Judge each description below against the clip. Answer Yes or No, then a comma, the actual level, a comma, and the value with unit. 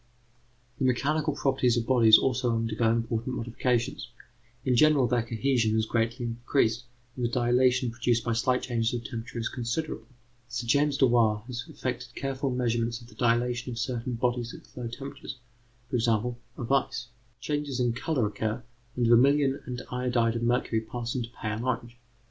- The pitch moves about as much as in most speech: No, narrow, 1.7 semitones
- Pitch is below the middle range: Yes, low, 120 Hz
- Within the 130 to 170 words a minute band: Yes, average, 165 wpm